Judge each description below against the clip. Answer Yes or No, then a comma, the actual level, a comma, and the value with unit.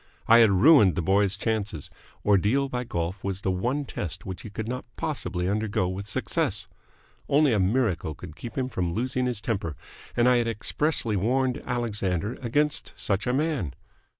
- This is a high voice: No, low, 110 Hz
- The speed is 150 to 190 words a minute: Yes, average, 175 wpm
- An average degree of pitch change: Yes, average, 5.0 semitones